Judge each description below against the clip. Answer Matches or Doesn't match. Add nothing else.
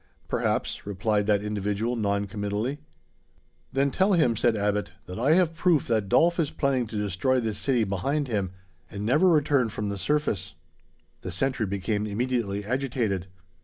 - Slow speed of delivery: Doesn't match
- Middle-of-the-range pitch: Doesn't match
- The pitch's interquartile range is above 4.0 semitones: Matches